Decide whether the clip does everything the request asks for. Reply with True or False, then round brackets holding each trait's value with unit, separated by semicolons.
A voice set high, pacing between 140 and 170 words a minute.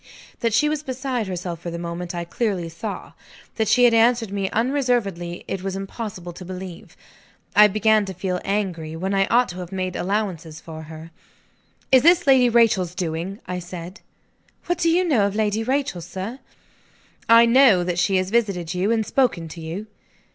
False (195 Hz; 185 wpm)